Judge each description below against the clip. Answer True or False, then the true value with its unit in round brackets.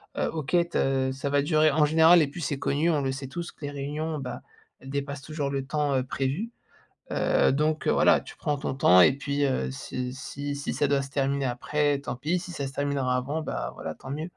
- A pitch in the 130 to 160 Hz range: True (140 Hz)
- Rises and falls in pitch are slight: True (2.2 semitones)